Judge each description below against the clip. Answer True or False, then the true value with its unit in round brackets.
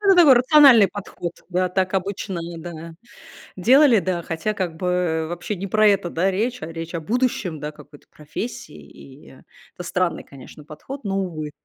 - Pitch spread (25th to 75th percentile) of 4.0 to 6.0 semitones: True (4.6 semitones)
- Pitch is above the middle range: False (180 Hz)